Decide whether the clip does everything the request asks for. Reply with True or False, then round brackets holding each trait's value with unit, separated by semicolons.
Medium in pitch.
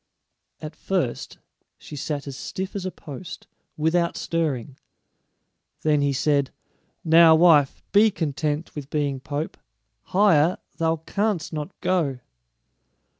True (155 Hz)